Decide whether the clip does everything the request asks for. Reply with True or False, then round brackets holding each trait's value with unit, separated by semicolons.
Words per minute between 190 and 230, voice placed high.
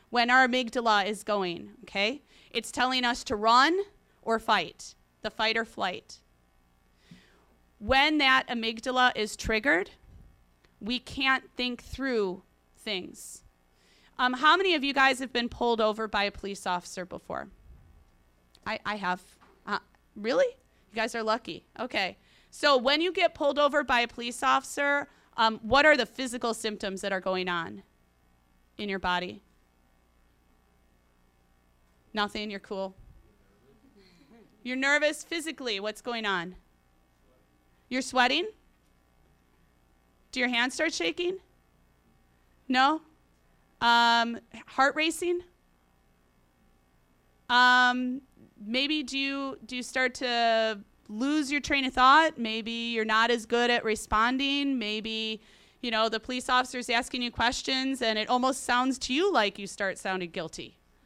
False (135 wpm; 225 Hz)